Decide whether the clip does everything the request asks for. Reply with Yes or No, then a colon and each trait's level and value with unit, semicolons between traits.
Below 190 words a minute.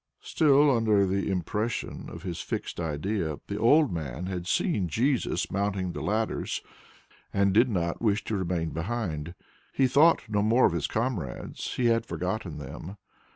Yes: average, 155 wpm